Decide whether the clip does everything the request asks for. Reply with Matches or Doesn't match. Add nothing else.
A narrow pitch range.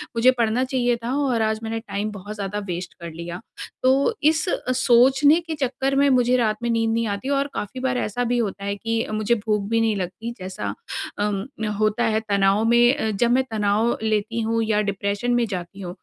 Doesn't match